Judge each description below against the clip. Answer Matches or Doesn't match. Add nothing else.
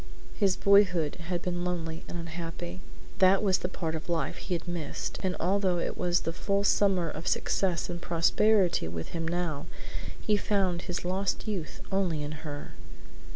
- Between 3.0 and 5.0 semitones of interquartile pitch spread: Doesn't match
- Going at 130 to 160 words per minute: Doesn't match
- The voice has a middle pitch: Matches